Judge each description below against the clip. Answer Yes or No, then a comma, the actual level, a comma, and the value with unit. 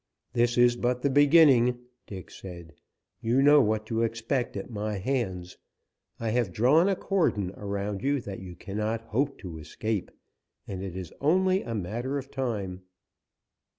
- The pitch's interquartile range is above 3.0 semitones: Yes, average, 5.2 semitones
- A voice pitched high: No, low, 115 Hz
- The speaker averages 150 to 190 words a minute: Yes, average, 155 wpm